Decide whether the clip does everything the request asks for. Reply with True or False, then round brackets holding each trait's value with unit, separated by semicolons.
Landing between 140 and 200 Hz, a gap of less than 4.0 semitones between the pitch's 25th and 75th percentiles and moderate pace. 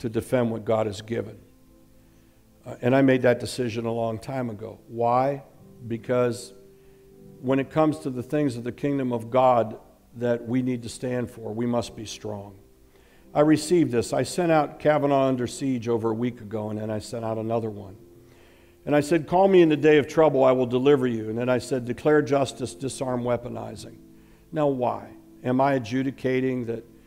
False (120 Hz; 2.9 semitones; 195 wpm)